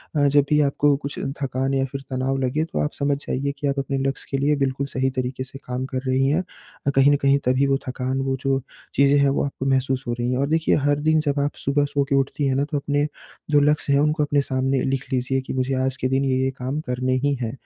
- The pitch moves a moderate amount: No, narrow, 1.6 semitones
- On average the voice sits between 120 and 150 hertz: Yes, low, 135 Hz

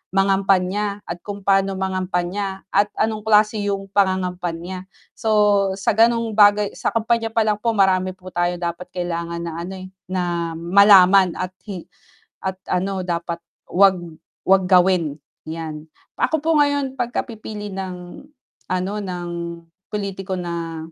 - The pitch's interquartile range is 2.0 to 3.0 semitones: Yes, narrow, 2.5 semitones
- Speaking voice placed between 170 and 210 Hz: Yes, high, 190 Hz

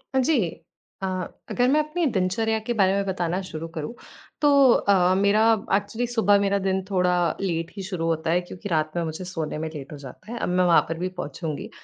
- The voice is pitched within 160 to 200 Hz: Yes, medium, 185 Hz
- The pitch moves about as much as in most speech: Yes, average, 3.6 semitones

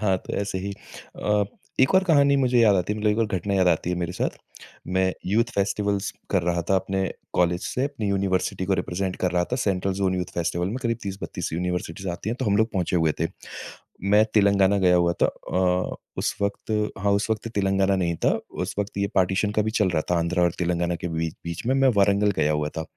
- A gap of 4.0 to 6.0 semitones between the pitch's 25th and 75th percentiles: No, average, 2.7 semitones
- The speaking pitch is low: Yes, very low, 95 Hz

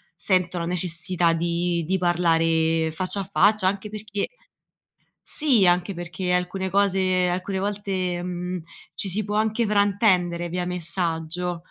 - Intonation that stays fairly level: Yes, narrow, 2.3 semitones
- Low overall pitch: No, medium, 180 Hz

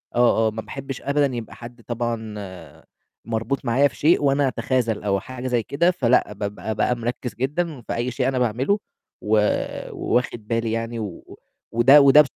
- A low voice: Yes, low, 120 Hz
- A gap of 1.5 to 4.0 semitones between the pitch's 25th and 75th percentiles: Yes, average, 3.0 semitones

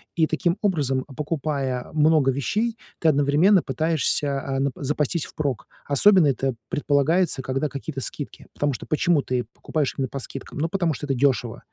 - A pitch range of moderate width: Yes, average, 3.0 semitones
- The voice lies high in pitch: No, medium, 145 Hz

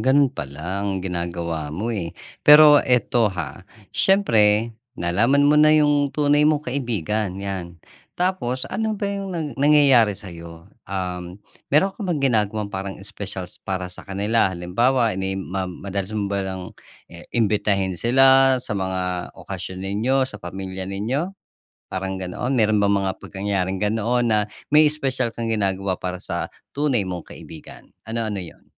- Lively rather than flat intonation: Yes, wide, 6.0 semitones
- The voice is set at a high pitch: No, low, 105 Hz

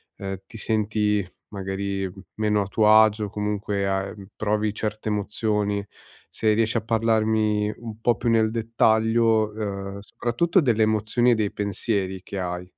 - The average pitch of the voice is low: Yes, low, 105 Hz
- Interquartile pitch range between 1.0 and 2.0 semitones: Yes, narrow, 1.7 semitones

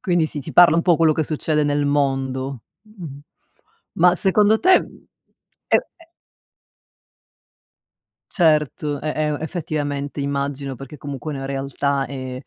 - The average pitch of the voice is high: No, medium, 145 Hz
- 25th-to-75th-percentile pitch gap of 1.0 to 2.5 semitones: No, average, 2.9 semitones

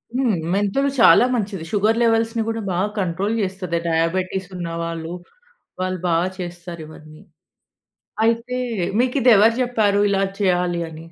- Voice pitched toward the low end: No, high, 190 Hz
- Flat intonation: No, average, 4.7 semitones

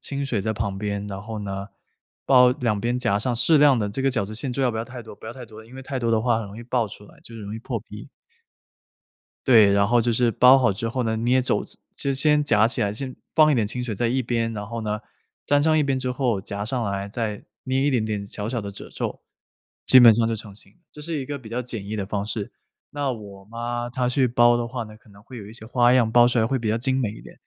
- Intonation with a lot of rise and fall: No, average, 3.1 semitones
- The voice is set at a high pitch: No, low, 115 Hz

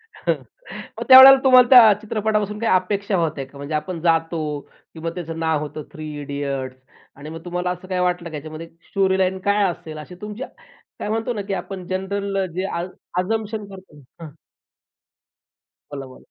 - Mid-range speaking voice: Yes, medium, 180 Hz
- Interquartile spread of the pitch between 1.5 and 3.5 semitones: No, average, 4.3 semitones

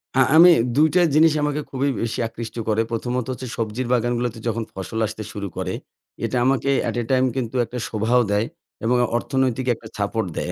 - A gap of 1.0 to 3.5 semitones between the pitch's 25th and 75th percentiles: Yes, average, 2.8 semitones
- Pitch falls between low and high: No, low, 120 Hz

